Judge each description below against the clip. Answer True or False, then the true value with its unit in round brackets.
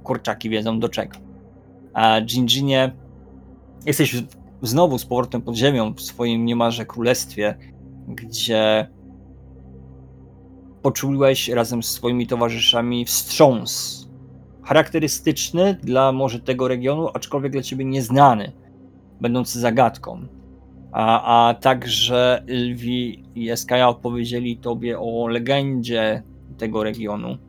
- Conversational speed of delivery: False (100 wpm)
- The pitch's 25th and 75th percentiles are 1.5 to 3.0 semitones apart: False (4.6 semitones)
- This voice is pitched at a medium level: False (120 Hz)